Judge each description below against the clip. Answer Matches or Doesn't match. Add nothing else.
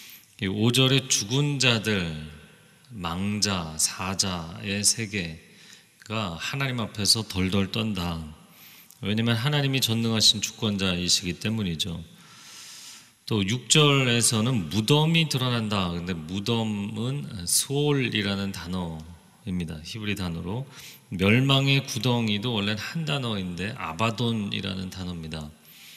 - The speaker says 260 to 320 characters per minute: Doesn't match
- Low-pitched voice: Matches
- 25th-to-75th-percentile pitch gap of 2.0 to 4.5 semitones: Doesn't match